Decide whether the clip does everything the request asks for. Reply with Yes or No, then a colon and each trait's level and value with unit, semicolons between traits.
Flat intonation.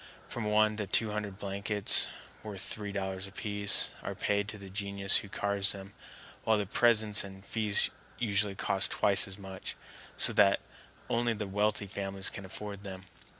Yes: narrow, 1.4 semitones